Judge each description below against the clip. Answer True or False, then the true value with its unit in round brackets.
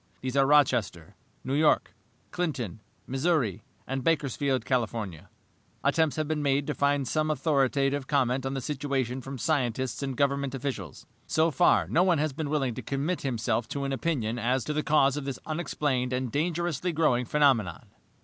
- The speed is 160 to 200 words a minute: True (170 wpm)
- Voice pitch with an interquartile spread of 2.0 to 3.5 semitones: True (3.0 semitones)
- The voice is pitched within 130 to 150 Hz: True (140 Hz)